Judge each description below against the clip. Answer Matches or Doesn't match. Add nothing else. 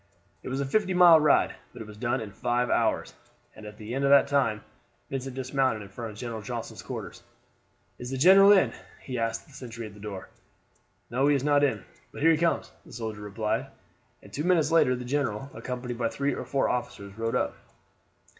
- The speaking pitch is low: Matches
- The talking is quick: Matches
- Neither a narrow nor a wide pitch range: Matches